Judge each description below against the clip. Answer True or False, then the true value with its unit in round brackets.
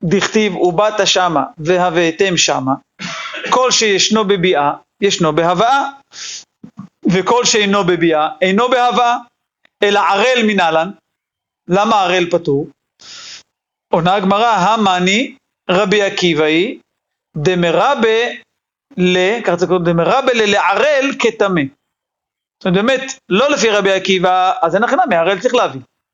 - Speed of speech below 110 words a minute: True (100 wpm)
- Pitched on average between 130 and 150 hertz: False (195 Hz)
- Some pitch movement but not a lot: True (4.2 semitones)